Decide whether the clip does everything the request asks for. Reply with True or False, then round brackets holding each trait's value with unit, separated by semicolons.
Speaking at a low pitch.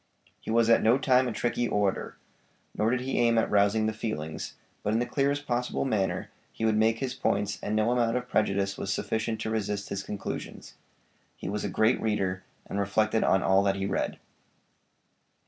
True (110 Hz)